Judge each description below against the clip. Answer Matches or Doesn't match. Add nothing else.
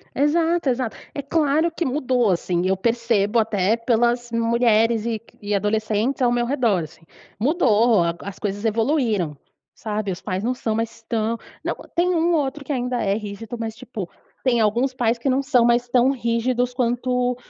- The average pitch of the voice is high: Matches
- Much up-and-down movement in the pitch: Doesn't match